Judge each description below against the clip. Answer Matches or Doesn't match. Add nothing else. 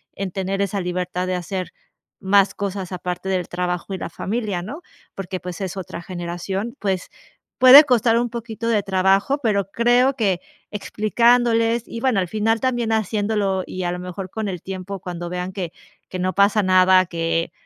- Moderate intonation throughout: Matches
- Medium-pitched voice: Doesn't match